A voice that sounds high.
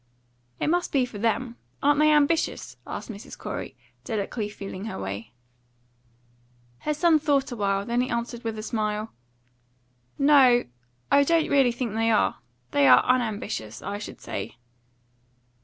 Yes: high, 235 Hz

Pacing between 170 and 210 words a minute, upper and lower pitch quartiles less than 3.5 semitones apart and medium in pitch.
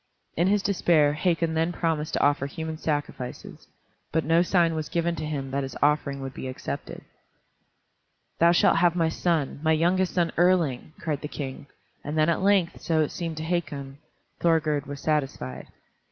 Yes: average, 175 wpm; average, 2.8 semitones; medium, 160 Hz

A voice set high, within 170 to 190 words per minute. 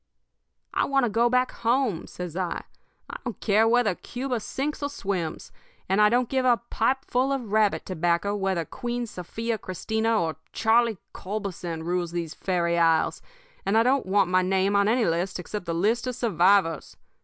Yes: high, 205 Hz; average, 175 wpm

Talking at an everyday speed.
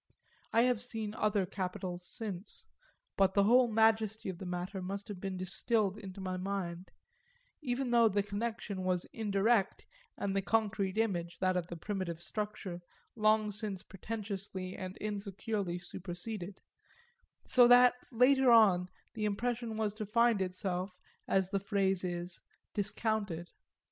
Yes: average, 145 wpm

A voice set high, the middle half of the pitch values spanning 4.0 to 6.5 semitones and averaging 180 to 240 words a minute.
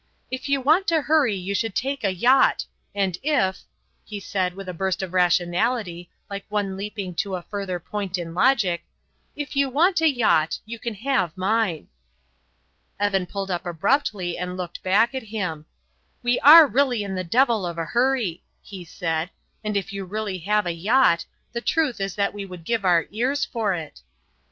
Yes: high, 200 Hz; average, 5.1 semitones; average, 185 wpm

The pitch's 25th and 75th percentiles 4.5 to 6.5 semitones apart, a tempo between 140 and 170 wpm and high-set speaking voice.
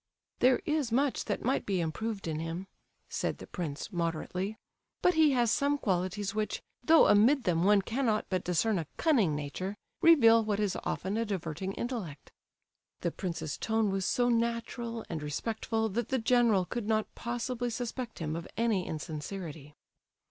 Yes: average, 5.2 semitones; average, 155 wpm; high, 210 Hz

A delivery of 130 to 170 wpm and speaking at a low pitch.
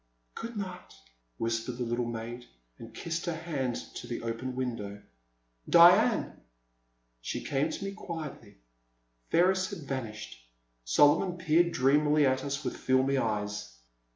Yes: slow, 135 wpm; low, 130 Hz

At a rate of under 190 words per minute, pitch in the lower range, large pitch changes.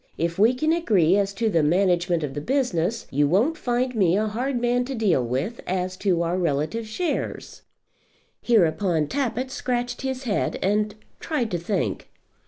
No: average, 170 wpm; high, 205 Hz; wide, 6.2 semitones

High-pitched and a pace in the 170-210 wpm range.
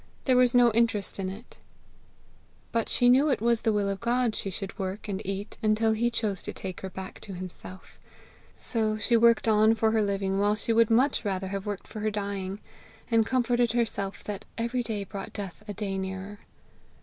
Yes: high, 215 Hz; average, 200 wpm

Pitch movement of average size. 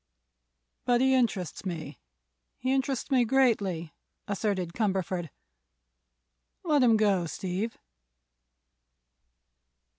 No: wide, 5.8 semitones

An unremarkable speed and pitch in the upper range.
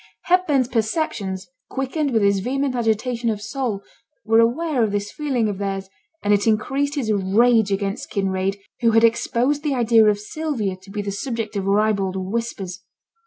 Yes: average, 165 wpm; high, 220 Hz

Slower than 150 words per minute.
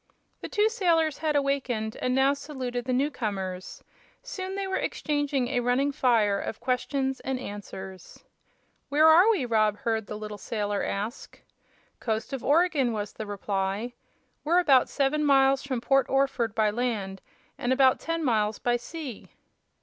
No: average, 155 wpm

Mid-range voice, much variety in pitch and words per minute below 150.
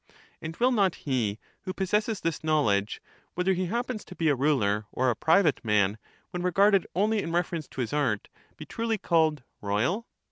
No: medium, 165 Hz; wide, 7.7 semitones; fast, 205 wpm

